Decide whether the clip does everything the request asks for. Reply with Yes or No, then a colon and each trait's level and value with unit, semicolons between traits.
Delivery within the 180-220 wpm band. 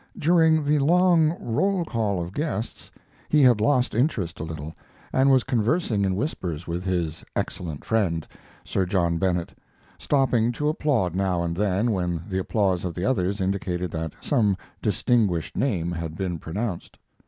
No: average, 155 wpm